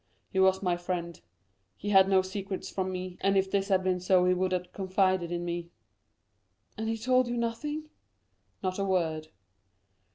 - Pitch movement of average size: No, narrow, 1.6 semitones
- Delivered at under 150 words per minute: No, average, 175 wpm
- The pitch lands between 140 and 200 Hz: Yes, high, 190 Hz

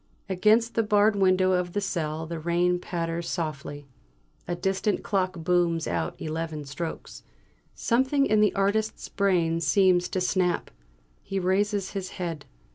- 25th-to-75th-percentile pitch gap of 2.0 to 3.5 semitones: Yes, average, 3.2 semitones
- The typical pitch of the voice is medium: Yes, medium, 180 Hz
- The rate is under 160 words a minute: Yes, average, 140 wpm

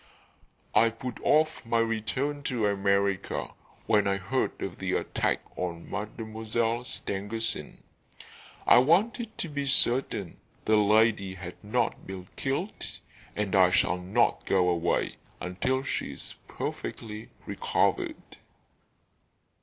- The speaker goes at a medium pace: No, slow, 115 wpm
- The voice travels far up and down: No, average, 4.3 semitones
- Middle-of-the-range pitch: No, low, 110 Hz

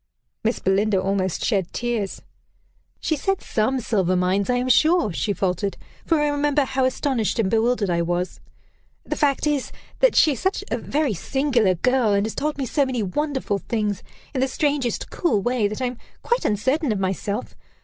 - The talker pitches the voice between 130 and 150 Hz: No, high, 240 Hz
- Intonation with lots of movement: Yes, wide, 5.9 semitones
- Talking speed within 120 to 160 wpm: No, average, 185 wpm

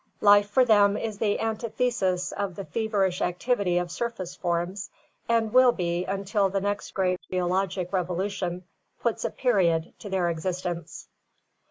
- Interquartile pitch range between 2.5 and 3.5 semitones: Yes, average, 3.0 semitones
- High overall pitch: Yes, high, 195 Hz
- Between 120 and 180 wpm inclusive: Yes, average, 145 wpm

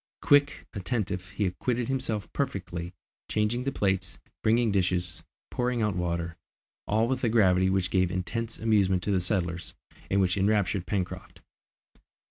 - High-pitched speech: No, low, 100 Hz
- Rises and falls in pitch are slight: No, average, 3.8 semitones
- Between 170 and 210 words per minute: No, average, 140 wpm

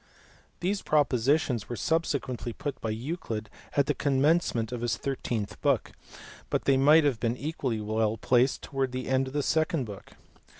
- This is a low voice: Yes, low, 130 Hz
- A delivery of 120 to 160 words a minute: No, average, 175 wpm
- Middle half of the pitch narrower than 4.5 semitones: Yes, average, 4.1 semitones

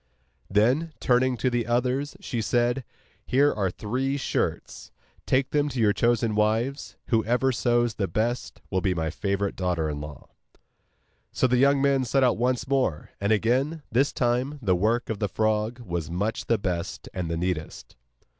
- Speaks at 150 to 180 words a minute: Yes, average, 170 wpm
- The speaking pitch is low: Yes, low, 120 Hz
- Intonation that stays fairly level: No, average, 4.4 semitones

